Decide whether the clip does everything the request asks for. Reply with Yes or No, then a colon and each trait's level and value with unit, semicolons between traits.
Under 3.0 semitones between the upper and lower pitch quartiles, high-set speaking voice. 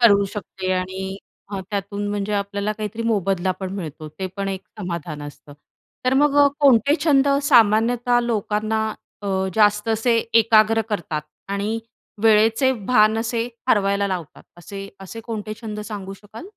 Yes: narrow, 2.6 semitones; high, 210 Hz